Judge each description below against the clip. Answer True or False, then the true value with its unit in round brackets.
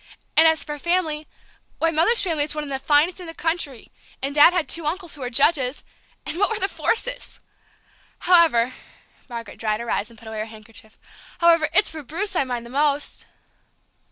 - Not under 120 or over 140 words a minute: False (190 wpm)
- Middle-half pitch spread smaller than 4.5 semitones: False (5.2 semitones)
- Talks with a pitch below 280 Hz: False (300 Hz)